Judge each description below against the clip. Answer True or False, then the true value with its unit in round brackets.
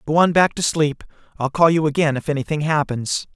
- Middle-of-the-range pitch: True (150 Hz)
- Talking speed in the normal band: False (215 wpm)